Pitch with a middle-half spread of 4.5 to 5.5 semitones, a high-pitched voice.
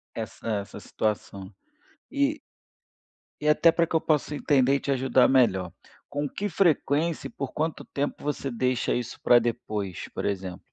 No: average, 5.0 semitones; low, 135 Hz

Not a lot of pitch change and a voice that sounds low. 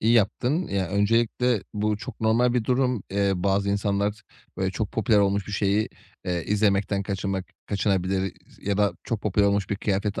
Yes: narrow, 1.9 semitones; low, 100 Hz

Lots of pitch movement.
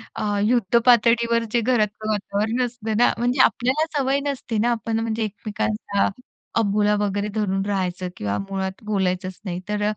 No: average, 2.8 semitones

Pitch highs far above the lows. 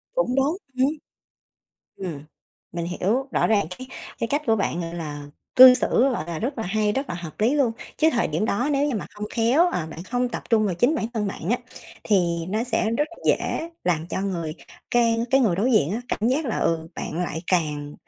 Yes: wide, 6.6 semitones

